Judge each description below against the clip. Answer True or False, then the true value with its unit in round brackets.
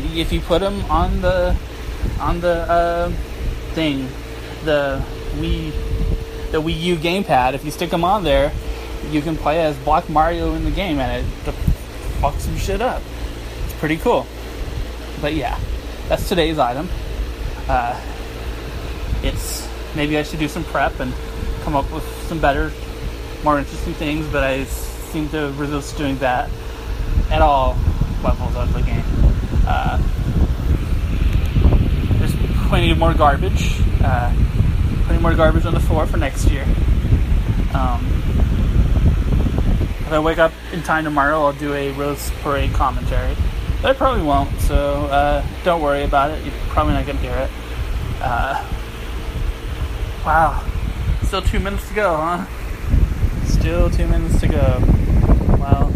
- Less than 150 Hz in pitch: True (135 Hz)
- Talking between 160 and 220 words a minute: False (145 wpm)